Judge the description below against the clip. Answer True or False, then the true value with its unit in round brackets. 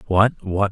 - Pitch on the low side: True (100 Hz)